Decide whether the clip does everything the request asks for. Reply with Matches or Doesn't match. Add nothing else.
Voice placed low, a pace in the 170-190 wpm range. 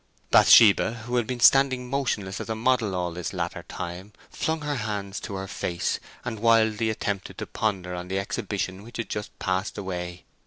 Matches